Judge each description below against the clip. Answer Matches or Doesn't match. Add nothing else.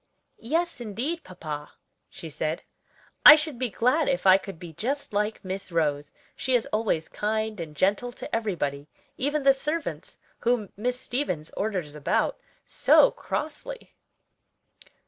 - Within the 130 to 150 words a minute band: Matches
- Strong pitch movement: Matches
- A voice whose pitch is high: Matches